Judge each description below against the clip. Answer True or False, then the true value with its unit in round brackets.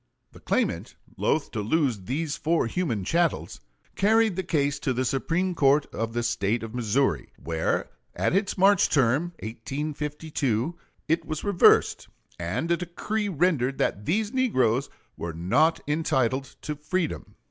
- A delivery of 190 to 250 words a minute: False (145 wpm)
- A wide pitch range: True (6.3 semitones)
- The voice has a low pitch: False (145 Hz)